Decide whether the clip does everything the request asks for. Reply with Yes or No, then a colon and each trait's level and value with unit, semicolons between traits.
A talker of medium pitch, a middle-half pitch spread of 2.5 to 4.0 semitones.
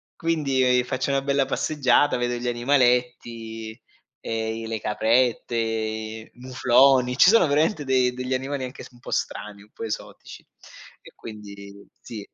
No: low, 125 Hz; average, 2.9 semitones